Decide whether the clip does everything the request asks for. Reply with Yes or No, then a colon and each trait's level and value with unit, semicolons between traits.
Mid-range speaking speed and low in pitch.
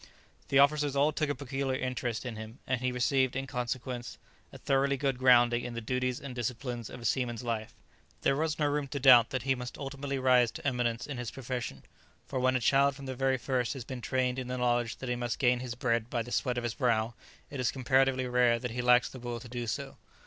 No: fast, 240 wpm; low, 125 Hz